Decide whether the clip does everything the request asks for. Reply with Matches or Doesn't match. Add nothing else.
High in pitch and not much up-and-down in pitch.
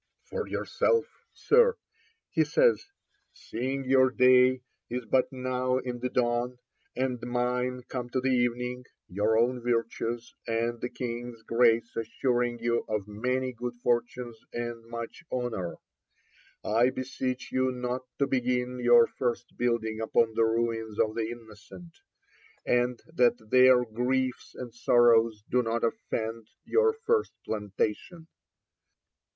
Doesn't match